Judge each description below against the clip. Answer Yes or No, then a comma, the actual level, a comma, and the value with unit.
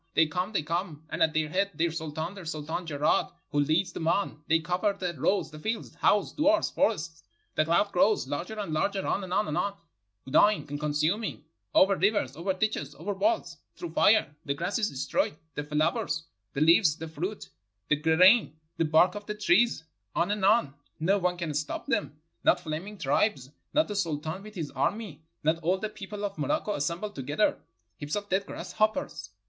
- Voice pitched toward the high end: No, medium, 175 Hz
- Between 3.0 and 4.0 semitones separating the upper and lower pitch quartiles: No, average, 4.9 semitones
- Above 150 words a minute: Yes, average, 185 wpm